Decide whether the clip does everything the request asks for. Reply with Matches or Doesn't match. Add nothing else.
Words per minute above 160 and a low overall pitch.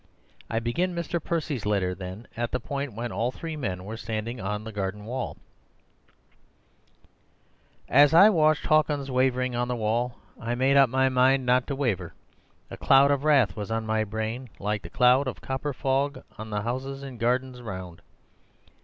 Matches